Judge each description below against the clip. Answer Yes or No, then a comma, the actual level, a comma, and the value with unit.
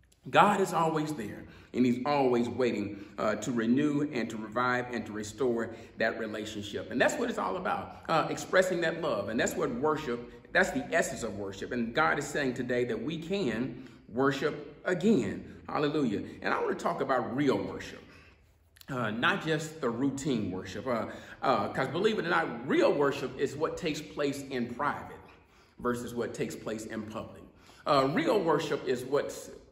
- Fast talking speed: No, average, 180 wpm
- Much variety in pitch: Yes, wide, 5.7 semitones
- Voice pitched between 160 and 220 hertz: No, low, 125 Hz